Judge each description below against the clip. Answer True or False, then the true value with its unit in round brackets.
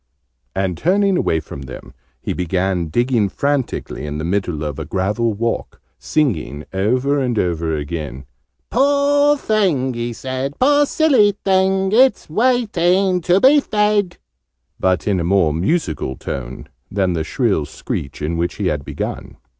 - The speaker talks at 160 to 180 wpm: False (145 wpm)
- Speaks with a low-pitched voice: True (115 Hz)